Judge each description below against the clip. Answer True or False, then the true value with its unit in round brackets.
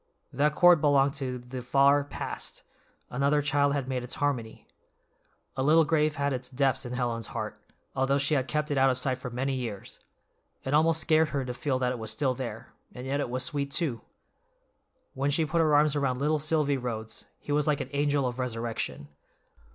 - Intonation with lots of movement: False (2.7 semitones)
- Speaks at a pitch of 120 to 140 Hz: True (135 Hz)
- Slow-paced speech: False (200 wpm)